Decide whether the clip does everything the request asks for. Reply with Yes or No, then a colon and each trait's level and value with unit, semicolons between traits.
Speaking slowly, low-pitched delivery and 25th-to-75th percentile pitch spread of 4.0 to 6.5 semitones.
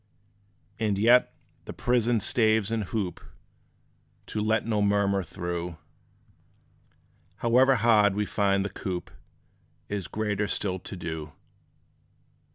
No: slow, 110 wpm; low, 105 Hz; narrow, 2.5 semitones